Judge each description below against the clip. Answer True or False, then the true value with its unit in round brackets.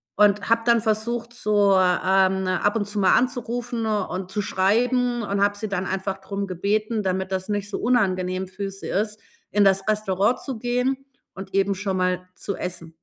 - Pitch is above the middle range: True (200 Hz)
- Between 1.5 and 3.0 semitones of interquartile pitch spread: True (2.6 semitones)